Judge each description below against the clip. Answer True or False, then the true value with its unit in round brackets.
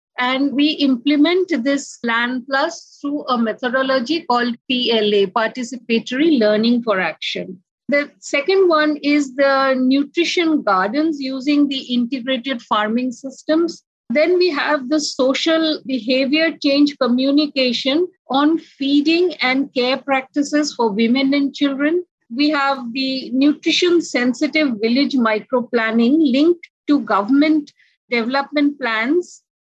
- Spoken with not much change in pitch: False (3.2 semitones)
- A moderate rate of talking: False (115 wpm)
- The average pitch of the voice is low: False (275 Hz)